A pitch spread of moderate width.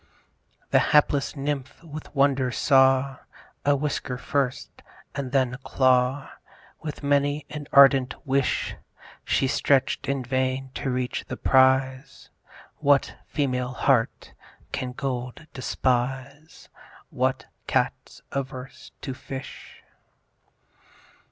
No: narrow, 1.4 semitones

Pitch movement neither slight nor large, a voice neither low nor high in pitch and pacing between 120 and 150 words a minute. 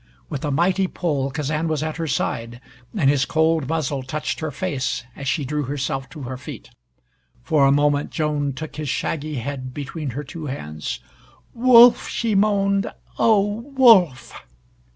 No: average, 3.6 semitones; medium, 150 Hz; average, 160 wpm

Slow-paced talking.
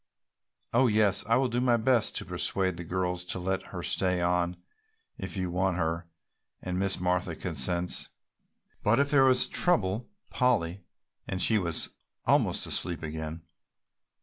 No: average, 155 wpm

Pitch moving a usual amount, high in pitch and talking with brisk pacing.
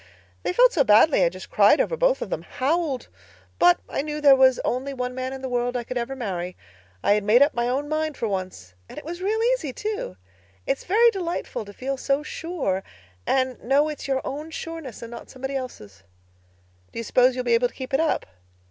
Yes: average, 4.4 semitones; very high, 265 Hz; fast, 220 wpm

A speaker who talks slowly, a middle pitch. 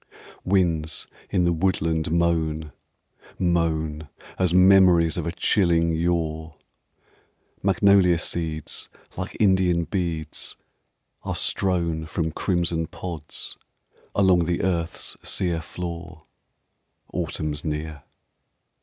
No: slow, 90 wpm; very low, 85 Hz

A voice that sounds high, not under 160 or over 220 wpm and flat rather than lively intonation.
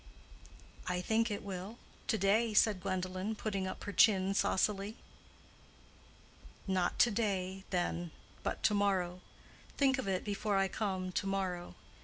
No: high, 195 Hz; average, 140 wpm; narrow, 2.3 semitones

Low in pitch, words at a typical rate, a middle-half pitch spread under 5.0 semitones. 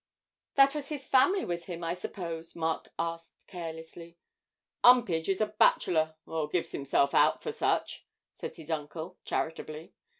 No: medium, 170 Hz; average, 145 wpm; average, 3.2 semitones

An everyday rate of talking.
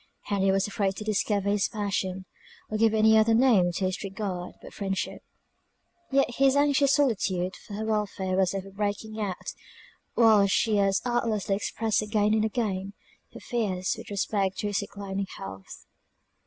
Yes: average, 160 wpm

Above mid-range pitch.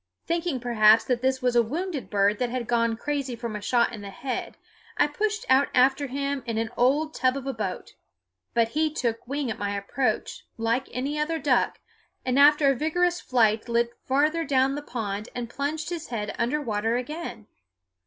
Yes: very high, 255 Hz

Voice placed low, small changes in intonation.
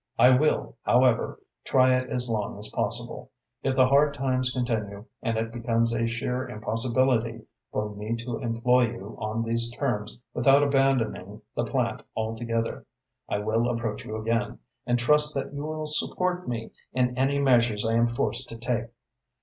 Yes: low, 120 Hz; narrow, 2.3 semitones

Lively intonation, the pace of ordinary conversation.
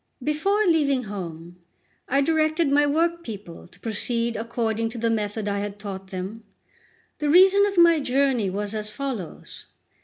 Yes: wide, 6.6 semitones; average, 155 wpm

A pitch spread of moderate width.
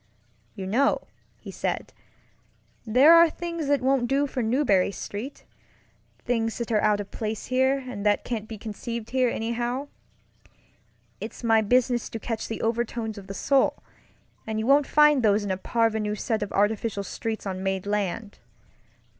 Yes: average, 3.5 semitones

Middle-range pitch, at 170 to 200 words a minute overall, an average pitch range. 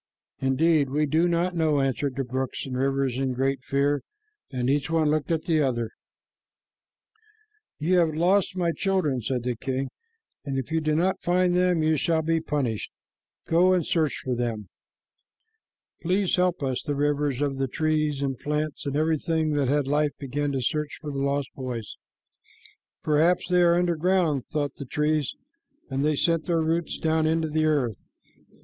Yes: medium, 150 Hz; average, 175 wpm; average, 3.3 semitones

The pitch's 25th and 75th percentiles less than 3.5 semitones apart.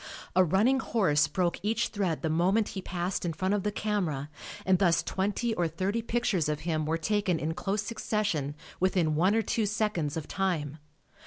No: average, 4.4 semitones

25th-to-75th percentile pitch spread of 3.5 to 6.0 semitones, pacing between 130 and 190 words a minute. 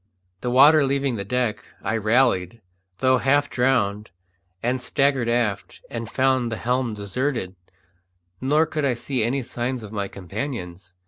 Yes: average, 3.8 semitones; average, 145 wpm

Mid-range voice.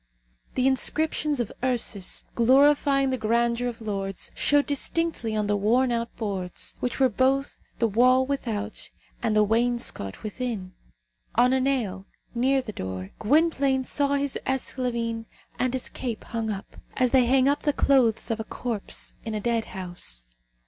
No: high, 240 Hz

